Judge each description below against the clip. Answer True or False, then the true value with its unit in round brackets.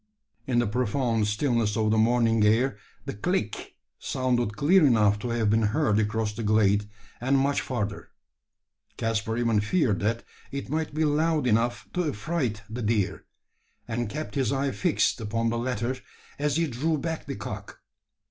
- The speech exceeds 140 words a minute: True (165 wpm)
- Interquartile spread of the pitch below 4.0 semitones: False (4.4 semitones)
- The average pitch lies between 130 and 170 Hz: False (120 Hz)